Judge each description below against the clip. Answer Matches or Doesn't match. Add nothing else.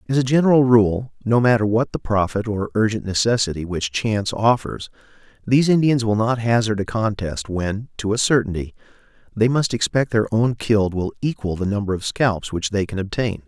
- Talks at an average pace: Matches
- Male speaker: Matches